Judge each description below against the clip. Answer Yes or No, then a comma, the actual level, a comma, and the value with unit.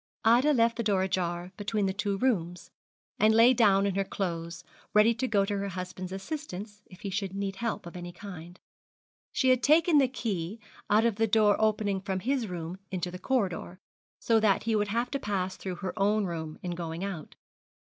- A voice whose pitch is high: Yes, high, 200 Hz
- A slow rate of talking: No, average, 200 wpm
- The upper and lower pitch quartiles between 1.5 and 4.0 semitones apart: Yes, average, 3.6 semitones